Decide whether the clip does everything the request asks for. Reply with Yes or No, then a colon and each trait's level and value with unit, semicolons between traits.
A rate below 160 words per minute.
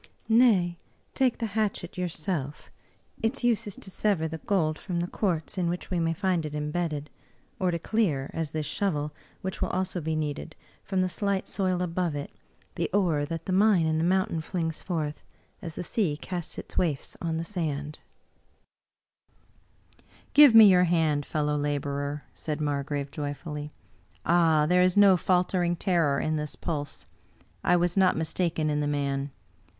No: average, 175 wpm